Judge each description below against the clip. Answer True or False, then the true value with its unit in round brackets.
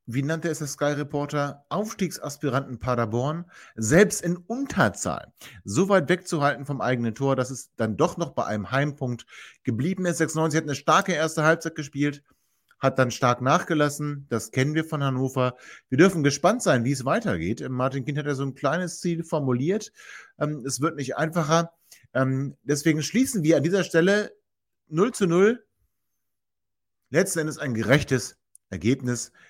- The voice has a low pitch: False (145 Hz)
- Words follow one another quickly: False (155 wpm)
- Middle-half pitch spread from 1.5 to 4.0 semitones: False (4.4 semitones)